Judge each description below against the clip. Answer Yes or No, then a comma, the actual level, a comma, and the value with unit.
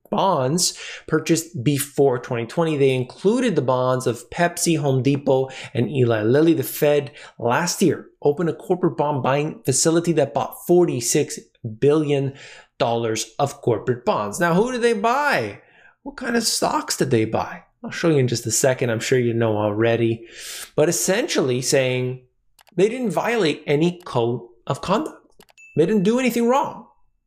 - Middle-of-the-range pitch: Yes, medium, 145 Hz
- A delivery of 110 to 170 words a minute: Yes, average, 155 wpm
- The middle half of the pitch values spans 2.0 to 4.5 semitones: No, wide, 5.5 semitones